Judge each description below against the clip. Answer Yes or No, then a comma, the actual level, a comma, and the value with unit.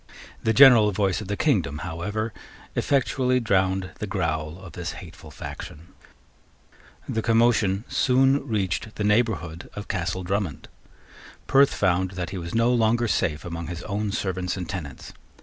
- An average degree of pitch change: Yes, average, 4.1 semitones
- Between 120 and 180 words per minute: Yes, average, 150 wpm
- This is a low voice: Yes, low, 100 Hz